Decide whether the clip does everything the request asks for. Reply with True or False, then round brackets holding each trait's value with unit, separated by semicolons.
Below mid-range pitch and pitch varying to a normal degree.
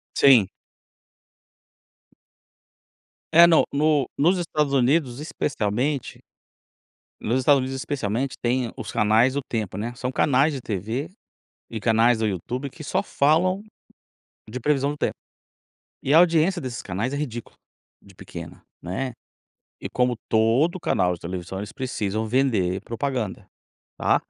True (125 Hz; 4.6 semitones)